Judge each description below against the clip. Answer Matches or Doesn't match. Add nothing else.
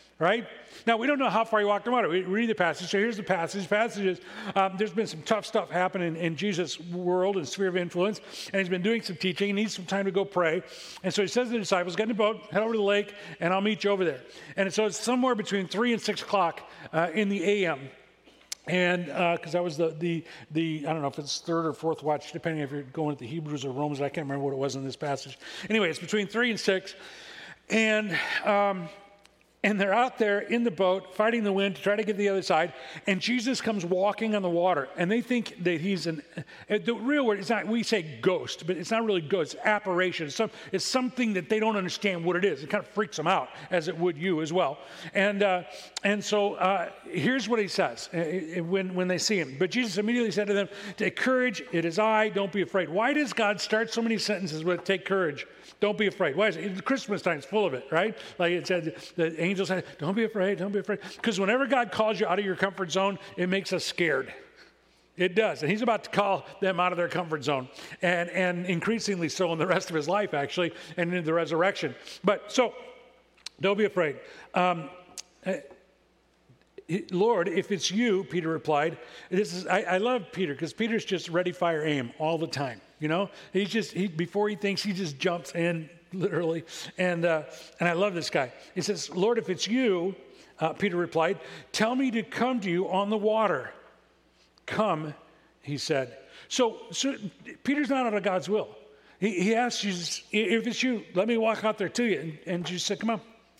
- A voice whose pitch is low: Doesn't match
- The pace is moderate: Doesn't match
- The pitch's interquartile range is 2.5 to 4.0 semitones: Matches